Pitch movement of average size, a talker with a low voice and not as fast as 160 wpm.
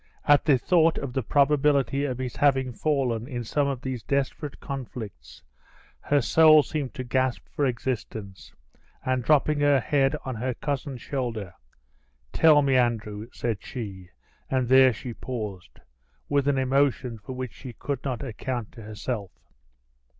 Yes: average, 3.1 semitones; low, 130 Hz; average, 150 wpm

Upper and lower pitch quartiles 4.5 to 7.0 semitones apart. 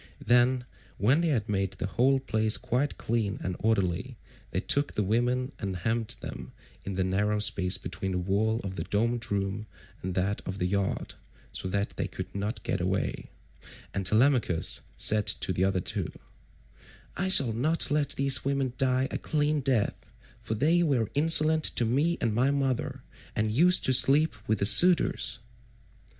Yes: wide, 5.5 semitones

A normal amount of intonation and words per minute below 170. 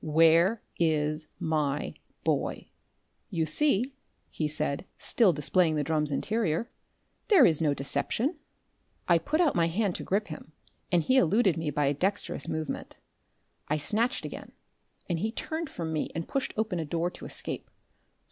No: wide, 6.0 semitones; average, 160 wpm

